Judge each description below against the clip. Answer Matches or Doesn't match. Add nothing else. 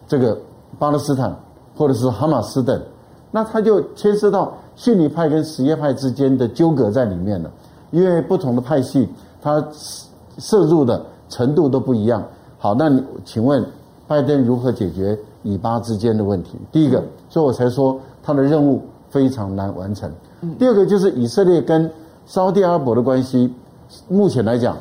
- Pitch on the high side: Doesn't match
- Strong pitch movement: Doesn't match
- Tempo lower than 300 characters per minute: Matches